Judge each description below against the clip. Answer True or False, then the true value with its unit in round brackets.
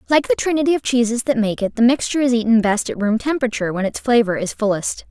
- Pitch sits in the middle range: False (235 Hz)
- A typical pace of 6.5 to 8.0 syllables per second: True (6.8 syllables/s)